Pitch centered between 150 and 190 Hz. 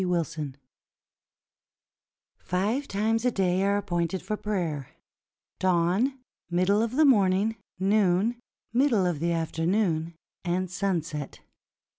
Yes: medium, 185 Hz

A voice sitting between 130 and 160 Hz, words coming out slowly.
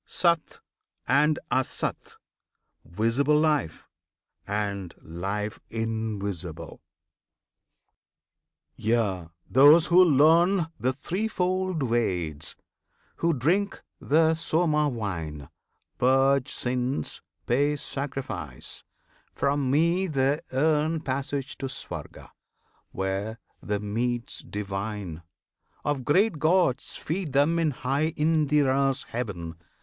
Yes: low, 135 Hz; slow, 90 wpm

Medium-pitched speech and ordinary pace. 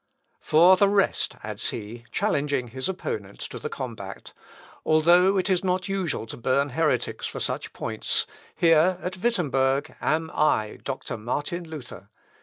Yes: medium, 155 Hz; average, 145 wpm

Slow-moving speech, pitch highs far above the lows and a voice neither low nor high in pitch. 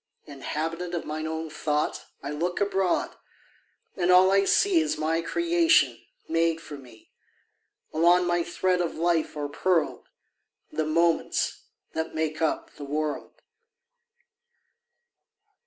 No: slow, 125 wpm; narrow, 2.5 semitones; medium, 165 Hz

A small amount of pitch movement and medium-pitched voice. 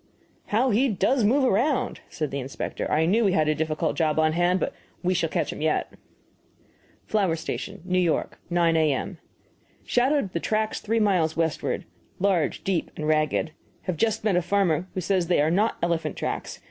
No: average, 4.7 semitones; medium, 180 Hz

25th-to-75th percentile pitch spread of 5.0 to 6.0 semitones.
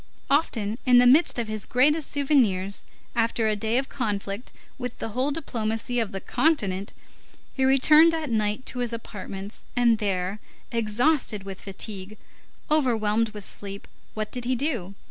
No: average, 3.9 semitones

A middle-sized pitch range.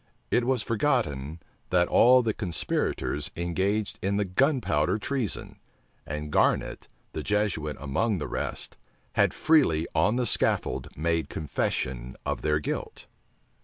No: wide, 6.9 semitones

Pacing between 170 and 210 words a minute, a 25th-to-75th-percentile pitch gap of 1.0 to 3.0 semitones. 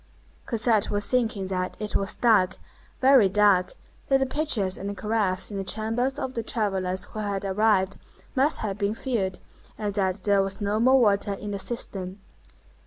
Yes: average, 175 wpm; average, 2.7 semitones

